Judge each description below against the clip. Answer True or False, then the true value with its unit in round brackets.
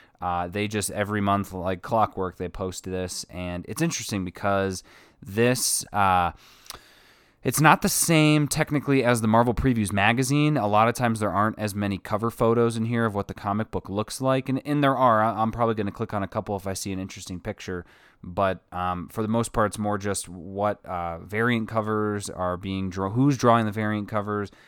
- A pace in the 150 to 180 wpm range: False (205 wpm)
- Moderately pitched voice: False (105 Hz)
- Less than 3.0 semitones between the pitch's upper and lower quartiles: False (3.3 semitones)